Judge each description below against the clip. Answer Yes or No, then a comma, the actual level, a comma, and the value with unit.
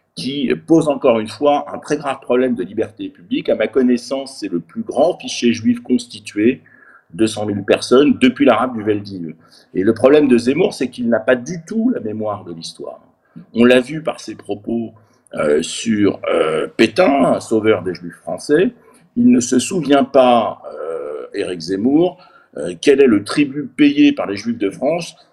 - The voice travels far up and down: Yes, wide, 6.6 semitones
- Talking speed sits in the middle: Yes, average, 180 wpm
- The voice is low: Yes, low, 125 Hz